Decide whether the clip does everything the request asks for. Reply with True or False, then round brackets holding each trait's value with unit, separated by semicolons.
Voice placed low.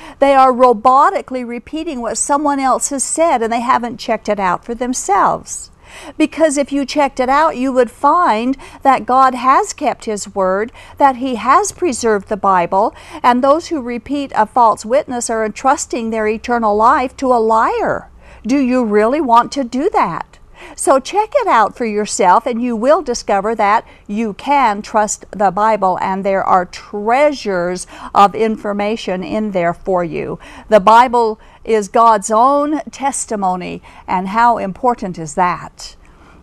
False (235 Hz)